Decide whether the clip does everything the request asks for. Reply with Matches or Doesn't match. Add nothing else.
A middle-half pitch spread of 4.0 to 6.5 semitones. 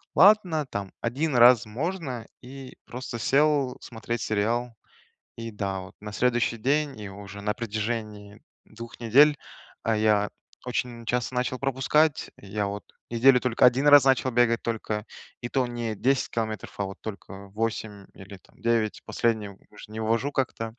Doesn't match